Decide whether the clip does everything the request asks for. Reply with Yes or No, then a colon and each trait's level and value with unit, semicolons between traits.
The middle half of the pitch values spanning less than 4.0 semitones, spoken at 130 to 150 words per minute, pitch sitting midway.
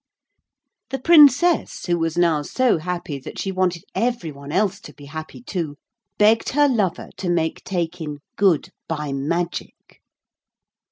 No: average, 5.1 semitones; average, 145 wpm; medium, 175 Hz